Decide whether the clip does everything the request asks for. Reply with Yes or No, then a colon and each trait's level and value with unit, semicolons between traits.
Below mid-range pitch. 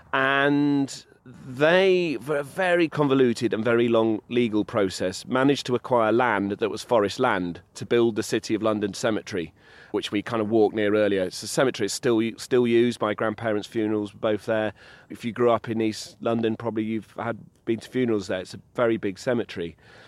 Yes: low, 115 Hz